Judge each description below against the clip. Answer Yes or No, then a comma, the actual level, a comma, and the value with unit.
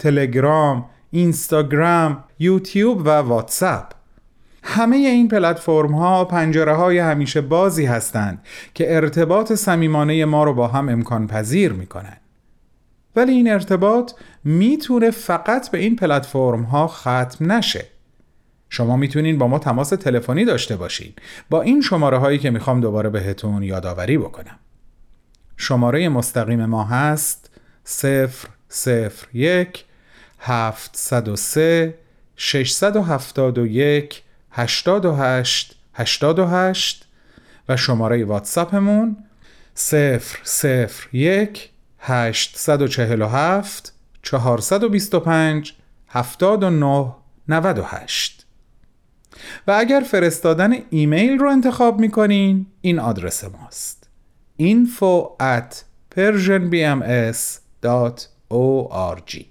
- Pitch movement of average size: No, wide, 7.2 semitones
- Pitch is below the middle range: No, medium, 150 Hz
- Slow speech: Yes, slow, 90 wpm